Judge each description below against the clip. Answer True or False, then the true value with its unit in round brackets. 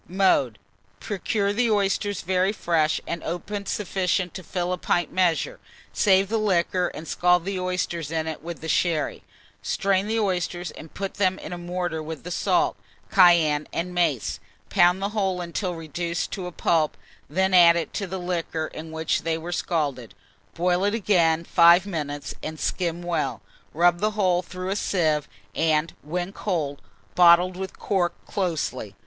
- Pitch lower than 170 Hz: False (175 Hz)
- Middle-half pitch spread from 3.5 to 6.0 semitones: False (2.6 semitones)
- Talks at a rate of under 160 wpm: False (165 wpm)